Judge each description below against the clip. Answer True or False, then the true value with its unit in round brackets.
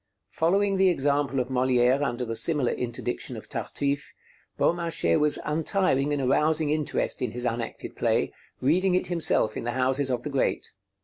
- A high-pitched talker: False (140 Hz)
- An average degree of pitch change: True (4.2 semitones)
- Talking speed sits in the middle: True (165 wpm)